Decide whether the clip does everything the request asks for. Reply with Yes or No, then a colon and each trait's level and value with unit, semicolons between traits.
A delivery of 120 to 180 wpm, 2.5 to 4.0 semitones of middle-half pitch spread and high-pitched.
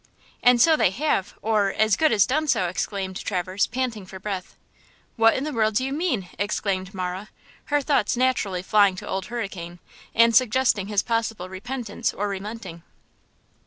No: average, 165 wpm; average, 4.5 semitones; high, 210 Hz